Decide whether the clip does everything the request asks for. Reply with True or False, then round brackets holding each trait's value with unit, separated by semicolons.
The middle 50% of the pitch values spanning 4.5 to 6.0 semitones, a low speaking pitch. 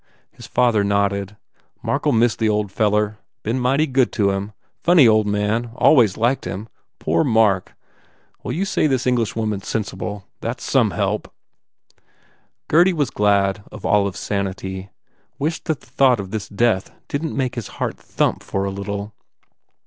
False (4.0 semitones; 110 Hz)